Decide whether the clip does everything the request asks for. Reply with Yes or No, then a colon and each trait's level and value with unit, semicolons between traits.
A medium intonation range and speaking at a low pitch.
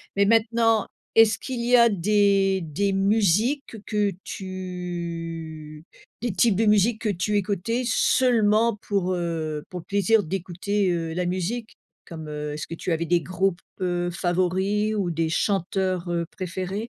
No: average, 3.6 semitones; high, 190 Hz